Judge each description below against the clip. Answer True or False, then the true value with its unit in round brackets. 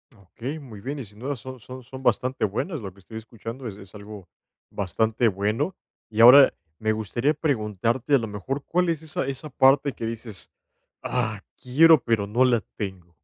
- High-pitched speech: False (115 Hz)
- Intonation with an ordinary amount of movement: True (4.2 semitones)